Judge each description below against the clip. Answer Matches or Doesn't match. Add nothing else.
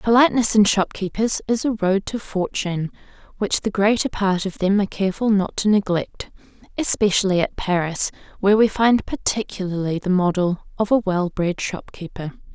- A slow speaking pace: Doesn't match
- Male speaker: Doesn't match